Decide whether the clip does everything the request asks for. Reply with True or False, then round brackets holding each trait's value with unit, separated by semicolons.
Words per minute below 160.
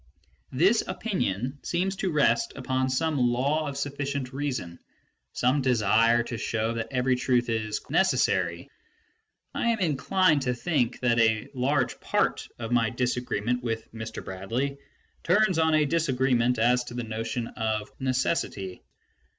True (150 wpm)